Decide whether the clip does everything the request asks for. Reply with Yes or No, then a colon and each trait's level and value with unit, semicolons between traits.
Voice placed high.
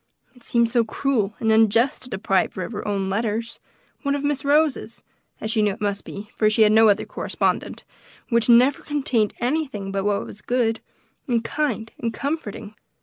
Yes: high, 225 Hz